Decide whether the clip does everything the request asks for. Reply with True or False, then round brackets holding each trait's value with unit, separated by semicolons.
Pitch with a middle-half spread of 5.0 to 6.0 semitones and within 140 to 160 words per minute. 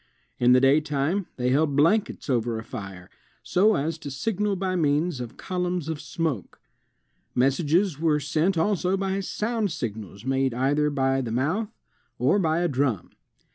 True (5.4 semitones; 155 wpm)